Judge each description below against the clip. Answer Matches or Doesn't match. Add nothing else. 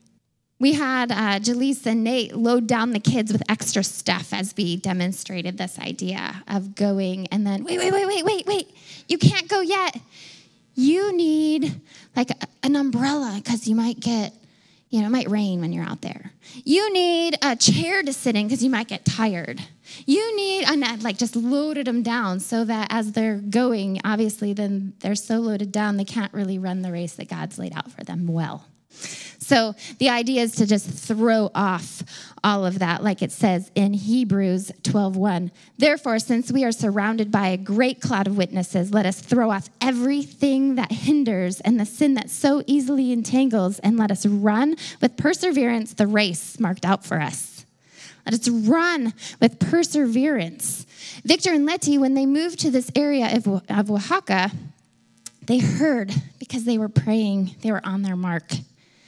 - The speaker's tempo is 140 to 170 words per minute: Doesn't match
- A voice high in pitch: Matches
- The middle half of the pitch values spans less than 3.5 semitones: Doesn't match